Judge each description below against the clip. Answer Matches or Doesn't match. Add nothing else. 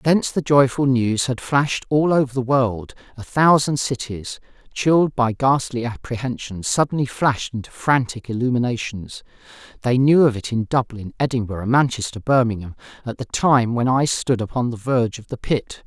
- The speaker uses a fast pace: Doesn't match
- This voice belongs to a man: Matches